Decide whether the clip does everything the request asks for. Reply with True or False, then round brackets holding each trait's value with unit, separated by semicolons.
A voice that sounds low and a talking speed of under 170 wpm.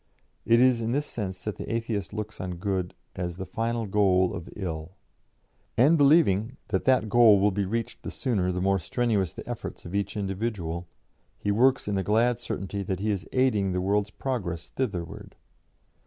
False (100 Hz; 185 wpm)